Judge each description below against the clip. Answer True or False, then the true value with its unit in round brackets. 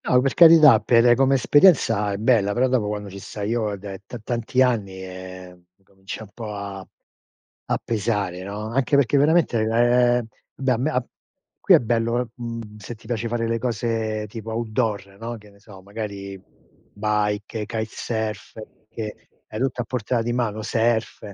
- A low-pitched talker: True (110 Hz)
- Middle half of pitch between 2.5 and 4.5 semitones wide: True (2.8 semitones)